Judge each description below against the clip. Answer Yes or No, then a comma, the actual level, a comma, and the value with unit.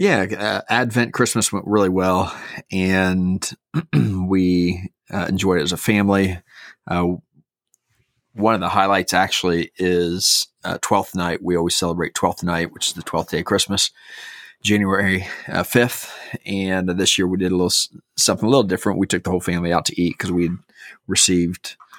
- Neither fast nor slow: Yes, average, 170 wpm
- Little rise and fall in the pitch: Yes, narrow, 2.2 semitones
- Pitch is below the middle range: Yes, very low, 95 Hz